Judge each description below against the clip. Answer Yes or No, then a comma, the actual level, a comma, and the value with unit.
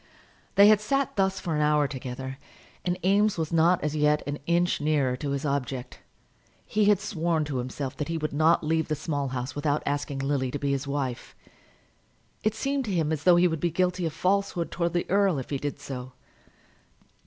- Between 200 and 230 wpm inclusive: Yes, fast, 205 wpm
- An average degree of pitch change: Yes, average, 4.0 semitones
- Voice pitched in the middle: Yes, medium, 155 Hz